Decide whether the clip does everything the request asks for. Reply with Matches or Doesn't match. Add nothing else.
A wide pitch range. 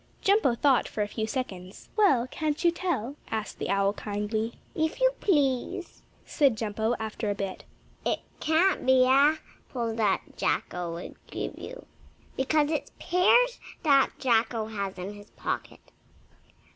Matches